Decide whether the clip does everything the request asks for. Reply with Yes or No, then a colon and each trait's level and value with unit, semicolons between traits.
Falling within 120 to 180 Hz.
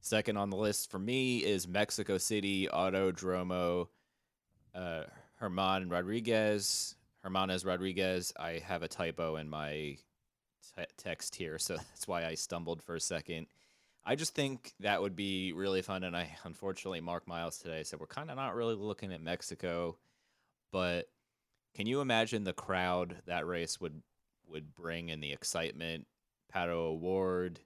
No: very low, 90 Hz